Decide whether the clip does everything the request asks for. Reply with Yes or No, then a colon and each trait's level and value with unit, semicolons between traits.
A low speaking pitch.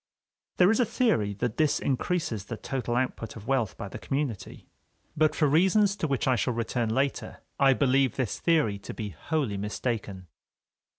Yes: low, 130 Hz